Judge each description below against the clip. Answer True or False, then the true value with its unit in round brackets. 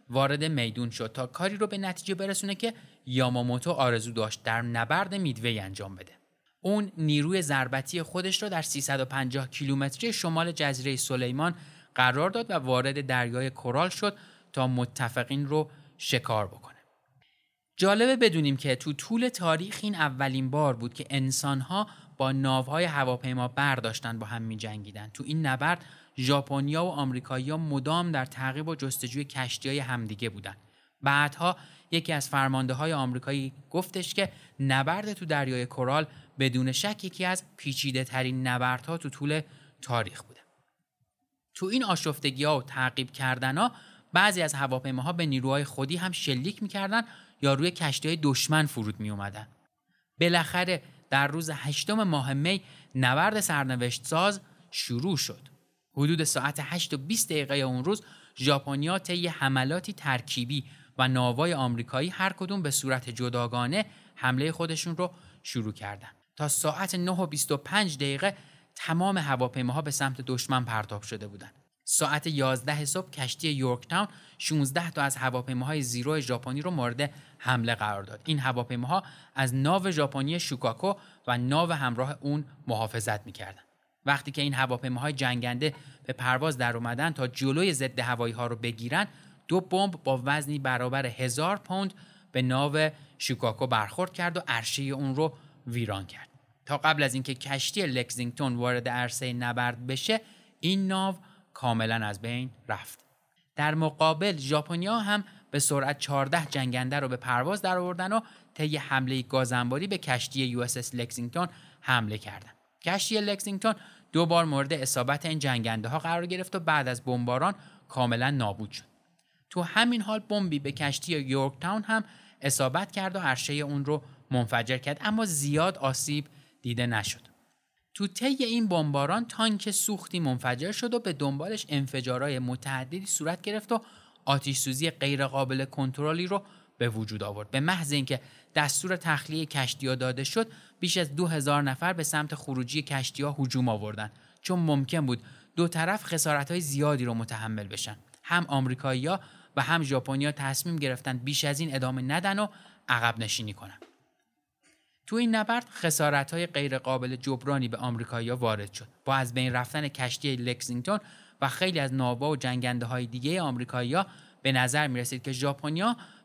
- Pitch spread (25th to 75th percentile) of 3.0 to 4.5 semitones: False (5.0 semitones)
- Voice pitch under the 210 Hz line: True (140 Hz)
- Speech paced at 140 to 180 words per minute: True (150 wpm)